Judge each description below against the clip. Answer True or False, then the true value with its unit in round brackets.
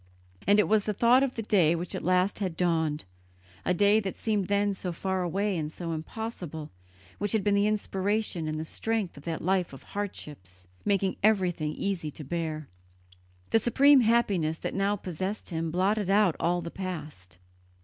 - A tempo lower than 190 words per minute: True (180 wpm)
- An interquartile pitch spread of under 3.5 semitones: False (4.2 semitones)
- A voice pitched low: False (185 Hz)